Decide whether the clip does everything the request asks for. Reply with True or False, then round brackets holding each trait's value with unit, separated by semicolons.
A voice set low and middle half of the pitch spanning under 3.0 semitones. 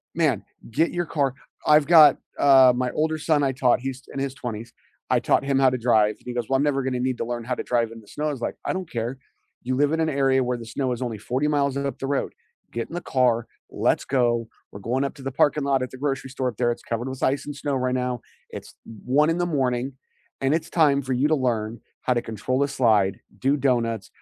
True (130 Hz; 2.6 semitones)